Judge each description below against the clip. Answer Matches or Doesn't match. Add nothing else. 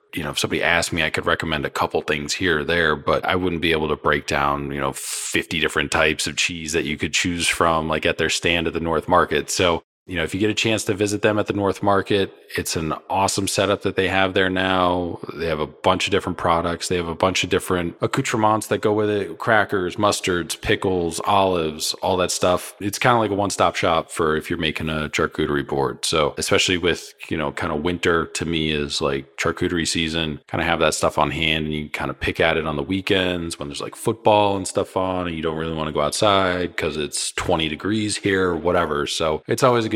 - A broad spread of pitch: Doesn't match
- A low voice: Matches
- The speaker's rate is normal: Doesn't match